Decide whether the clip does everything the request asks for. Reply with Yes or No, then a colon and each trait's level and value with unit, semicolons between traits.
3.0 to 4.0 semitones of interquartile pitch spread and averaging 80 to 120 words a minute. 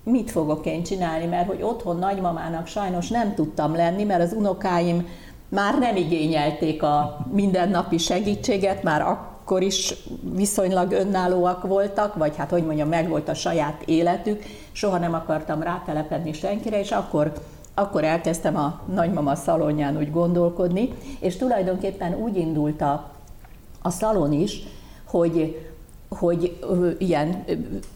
No: average, 3.5 semitones; average, 135 wpm